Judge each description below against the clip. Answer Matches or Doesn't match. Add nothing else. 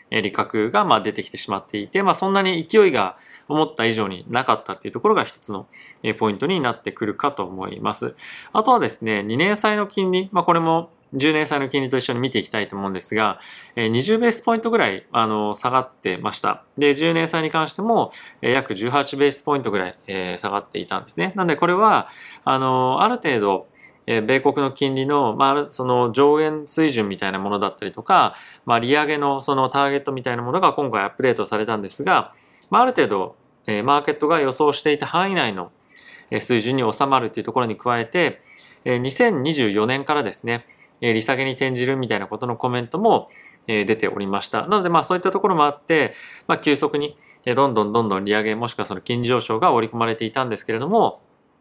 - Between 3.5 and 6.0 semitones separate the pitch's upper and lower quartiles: Matches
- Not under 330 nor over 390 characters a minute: Doesn't match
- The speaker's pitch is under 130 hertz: Doesn't match